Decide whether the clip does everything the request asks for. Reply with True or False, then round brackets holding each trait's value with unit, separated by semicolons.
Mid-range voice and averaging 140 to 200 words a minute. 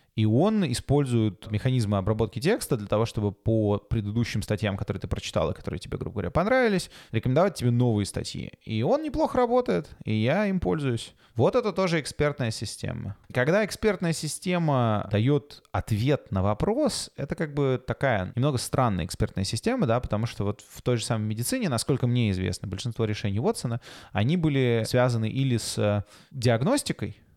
False (120 Hz; 160 wpm)